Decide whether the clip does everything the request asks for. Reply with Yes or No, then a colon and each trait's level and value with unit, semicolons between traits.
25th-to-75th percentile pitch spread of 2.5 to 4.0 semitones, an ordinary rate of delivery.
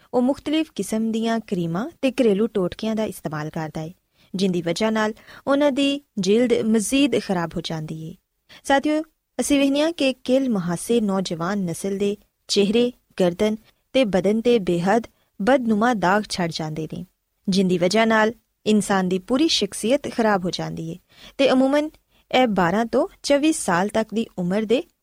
No: wide, 5.5 semitones; average, 155 wpm